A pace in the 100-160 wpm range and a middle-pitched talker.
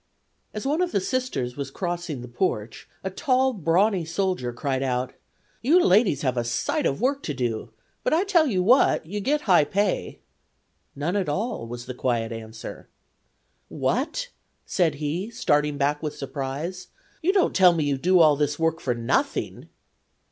No: average, 170 wpm; medium, 165 Hz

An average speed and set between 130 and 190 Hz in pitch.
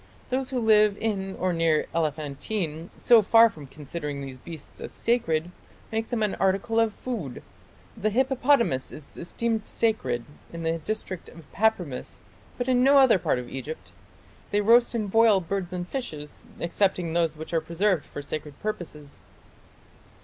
Yes: average, 155 wpm; medium, 185 Hz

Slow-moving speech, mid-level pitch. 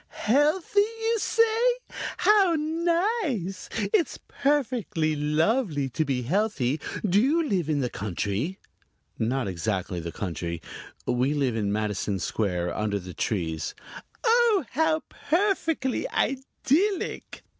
Yes: slow, 115 wpm; medium, 180 Hz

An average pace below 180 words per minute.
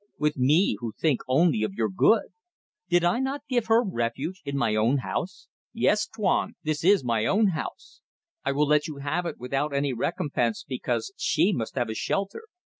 No: average, 190 wpm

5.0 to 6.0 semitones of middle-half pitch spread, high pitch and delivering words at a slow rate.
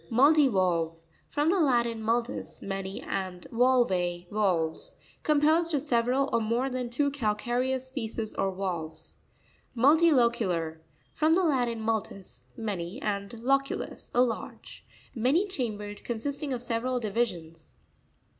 Yes: wide, 5.5 semitones; high, 235 Hz; slow, 115 wpm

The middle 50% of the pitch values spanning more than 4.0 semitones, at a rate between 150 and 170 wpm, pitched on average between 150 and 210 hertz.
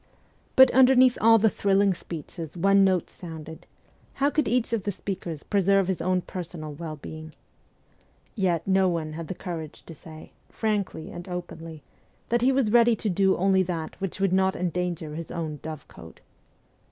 No: average, 3.6 semitones; average, 165 wpm; medium, 185 Hz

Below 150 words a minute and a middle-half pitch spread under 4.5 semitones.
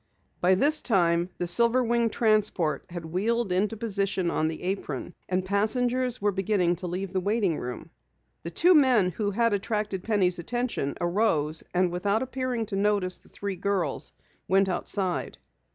No: average, 160 wpm; average, 4.1 semitones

